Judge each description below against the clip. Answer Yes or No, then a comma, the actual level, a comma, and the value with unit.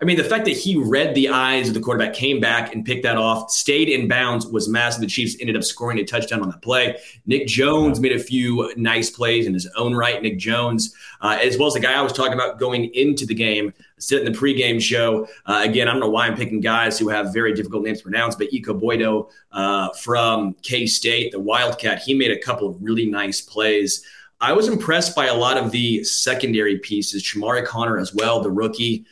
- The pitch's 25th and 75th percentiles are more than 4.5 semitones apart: No, average, 2.7 semitones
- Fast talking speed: Yes, fast, 235 wpm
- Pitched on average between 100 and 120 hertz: Yes, low, 115 Hz